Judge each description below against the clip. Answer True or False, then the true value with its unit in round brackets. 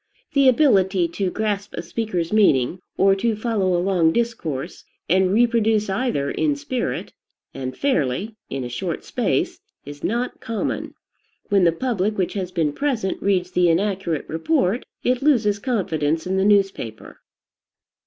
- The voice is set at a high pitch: True (195 Hz)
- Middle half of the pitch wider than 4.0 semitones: True (5.1 semitones)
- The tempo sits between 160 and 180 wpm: False (145 wpm)